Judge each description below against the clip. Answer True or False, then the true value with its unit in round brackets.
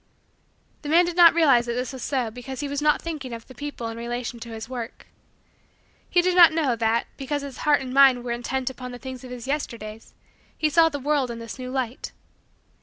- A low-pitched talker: False (260 Hz)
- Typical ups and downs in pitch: True (3.5 semitones)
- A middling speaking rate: False (230 wpm)